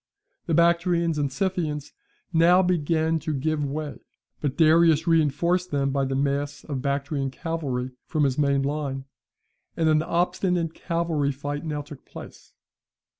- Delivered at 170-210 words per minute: No, average, 140 wpm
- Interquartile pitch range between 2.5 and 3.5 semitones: Yes, average, 3.1 semitones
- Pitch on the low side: No, medium, 155 Hz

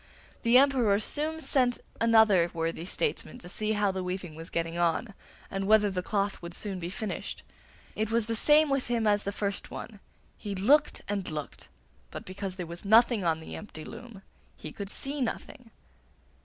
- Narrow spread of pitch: No, average, 4.3 semitones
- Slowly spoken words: No, average, 180 wpm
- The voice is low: No, high, 205 Hz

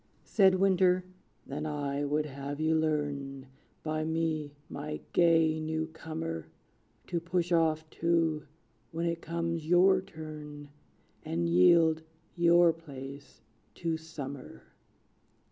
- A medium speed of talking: No, slow, 110 wpm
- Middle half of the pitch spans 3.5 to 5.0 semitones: No, narrow, 2.5 semitones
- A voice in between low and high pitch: Yes, medium, 160 Hz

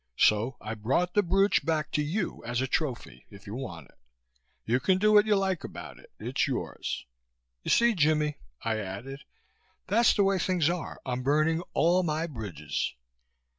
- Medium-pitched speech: Yes, medium, 150 Hz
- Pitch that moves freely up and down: Yes, wide, 7.4 semitones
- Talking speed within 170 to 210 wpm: Yes, average, 175 wpm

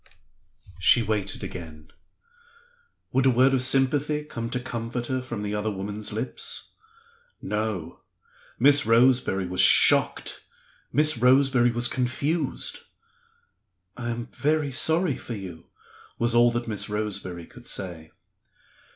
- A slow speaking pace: Yes, slow, 125 wpm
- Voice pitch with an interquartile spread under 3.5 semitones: No, average, 4.0 semitones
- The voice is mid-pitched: No, low, 120 Hz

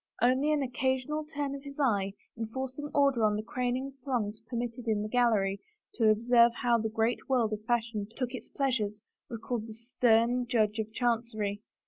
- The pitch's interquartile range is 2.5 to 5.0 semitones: Yes, average, 2.9 semitones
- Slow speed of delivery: No, average, 175 wpm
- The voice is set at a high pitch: Yes, high, 235 Hz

